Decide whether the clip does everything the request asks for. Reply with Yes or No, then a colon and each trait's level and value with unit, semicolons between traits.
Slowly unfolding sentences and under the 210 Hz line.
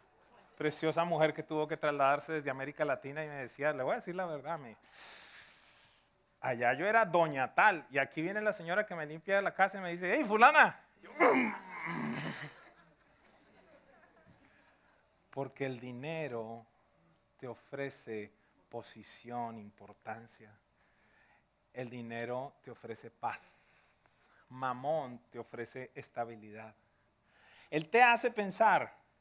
Yes: slow, 120 wpm; medium, 140 Hz